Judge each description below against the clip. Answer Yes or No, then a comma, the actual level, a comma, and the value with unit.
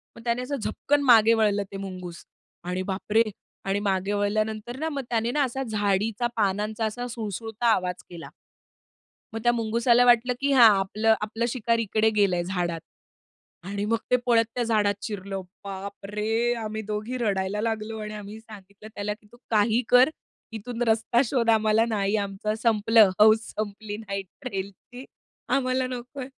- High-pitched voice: Yes, high, 215 Hz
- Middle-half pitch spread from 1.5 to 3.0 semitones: Yes, narrow, 2.6 semitones